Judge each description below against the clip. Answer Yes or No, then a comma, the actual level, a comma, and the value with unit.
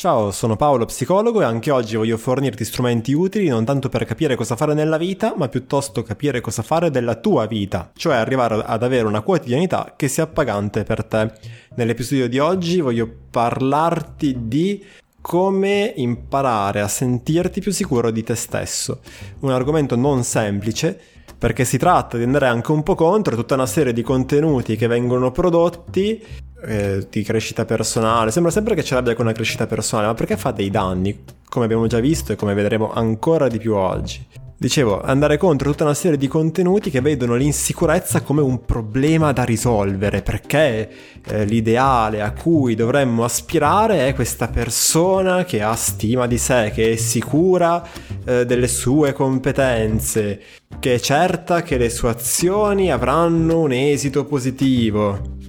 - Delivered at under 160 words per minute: No, average, 165 wpm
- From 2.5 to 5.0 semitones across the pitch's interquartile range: No, wide, 5.5 semitones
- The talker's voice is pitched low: Yes, low, 125 Hz